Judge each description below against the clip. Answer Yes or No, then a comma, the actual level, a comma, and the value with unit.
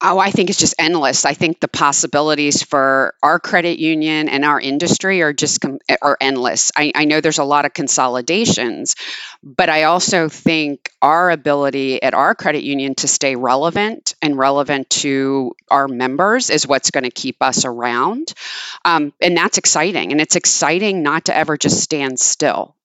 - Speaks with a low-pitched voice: No, medium, 150 Hz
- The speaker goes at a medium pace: Yes, average, 180 wpm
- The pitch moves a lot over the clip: No, average, 3.5 semitones